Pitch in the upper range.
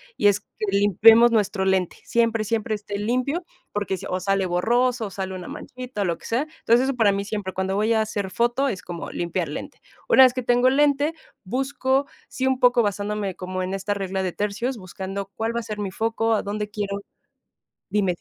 Yes: high, 210 Hz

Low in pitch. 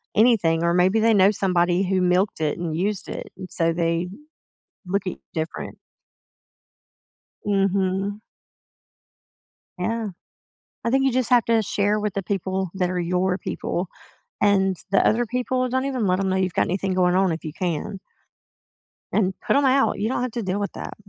No: high, 190 Hz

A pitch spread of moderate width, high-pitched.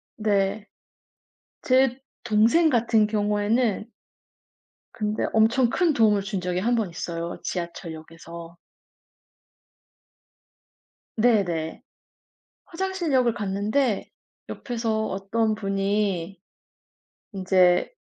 Yes: average, 3.7 semitones; high, 210 Hz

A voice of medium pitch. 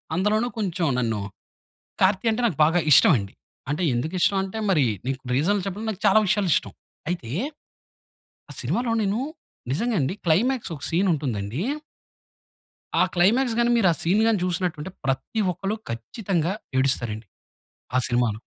Yes: medium, 180 Hz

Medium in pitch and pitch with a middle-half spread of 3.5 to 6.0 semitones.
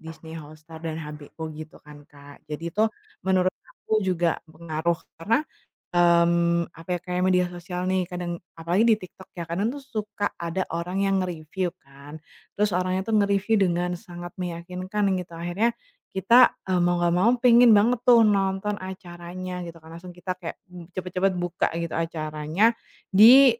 No: medium, 180 Hz; average, 2.7 semitones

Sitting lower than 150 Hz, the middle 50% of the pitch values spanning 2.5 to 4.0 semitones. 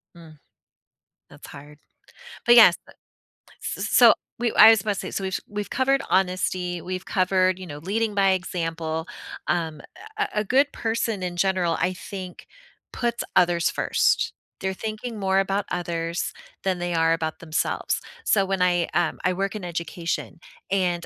No: medium, 185 Hz; average, 2.8 semitones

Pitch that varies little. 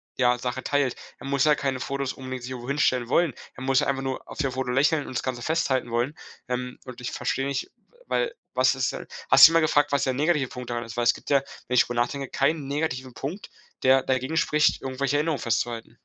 Yes: narrow, 2.2 semitones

